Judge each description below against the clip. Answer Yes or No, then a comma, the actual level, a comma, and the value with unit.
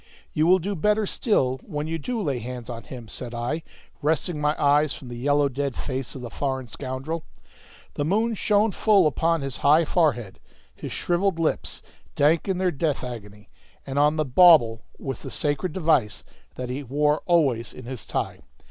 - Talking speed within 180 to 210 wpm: Yes, average, 185 wpm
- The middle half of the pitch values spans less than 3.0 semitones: No, average, 4.6 semitones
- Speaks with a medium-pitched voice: Yes, medium, 145 Hz